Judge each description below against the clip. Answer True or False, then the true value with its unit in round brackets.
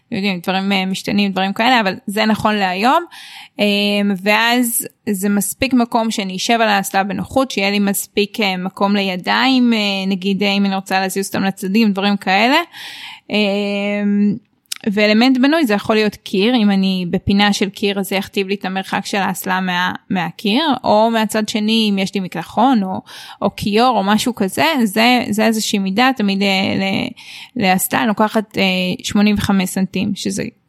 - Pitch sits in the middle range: False (205 Hz)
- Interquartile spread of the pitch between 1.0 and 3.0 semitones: True (2.4 semitones)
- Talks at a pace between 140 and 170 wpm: True (150 wpm)